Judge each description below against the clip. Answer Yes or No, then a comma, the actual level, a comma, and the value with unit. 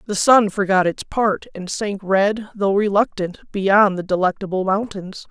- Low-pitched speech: No, high, 200 Hz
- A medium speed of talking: Yes, average, 160 wpm